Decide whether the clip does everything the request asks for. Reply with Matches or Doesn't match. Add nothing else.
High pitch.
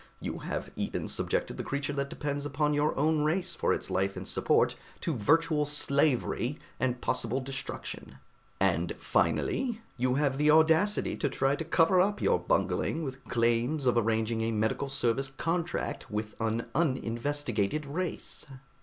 Doesn't match